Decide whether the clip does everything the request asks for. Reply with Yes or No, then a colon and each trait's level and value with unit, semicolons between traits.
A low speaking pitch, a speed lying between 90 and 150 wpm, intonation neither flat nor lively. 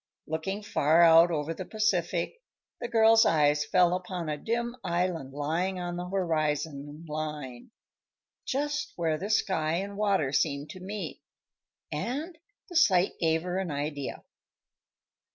No: medium, 175 Hz; slow, 135 wpm; average, 4.4 semitones